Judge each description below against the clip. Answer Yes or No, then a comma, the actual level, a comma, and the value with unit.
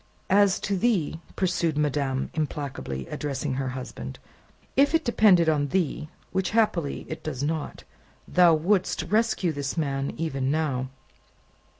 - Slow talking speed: Yes, slow, 130 wpm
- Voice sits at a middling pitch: Yes, medium, 155 Hz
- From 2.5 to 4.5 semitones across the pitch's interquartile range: No, average, 5.2 semitones